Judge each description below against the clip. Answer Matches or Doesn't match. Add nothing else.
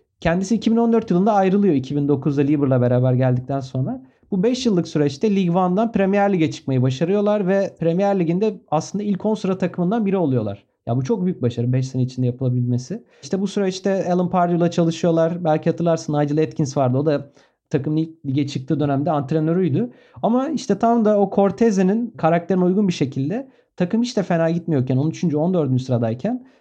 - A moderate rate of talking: Doesn't match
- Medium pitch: Matches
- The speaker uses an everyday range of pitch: Doesn't match